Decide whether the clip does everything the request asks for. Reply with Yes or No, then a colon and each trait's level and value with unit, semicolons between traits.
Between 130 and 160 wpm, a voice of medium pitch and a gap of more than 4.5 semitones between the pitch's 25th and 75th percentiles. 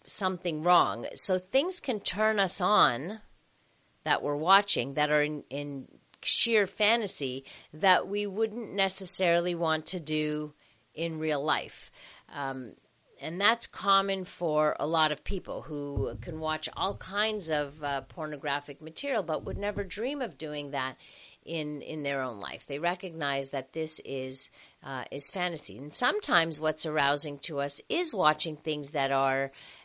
Yes: average, 155 wpm; medium, 155 Hz; average, 5.1 semitones